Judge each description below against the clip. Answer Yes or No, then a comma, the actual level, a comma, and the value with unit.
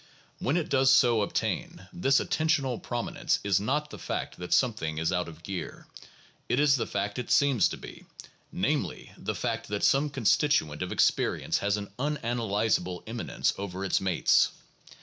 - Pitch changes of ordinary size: No, wide, 5.8 semitones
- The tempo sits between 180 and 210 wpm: No, average, 170 wpm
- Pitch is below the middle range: Yes, low, 115 Hz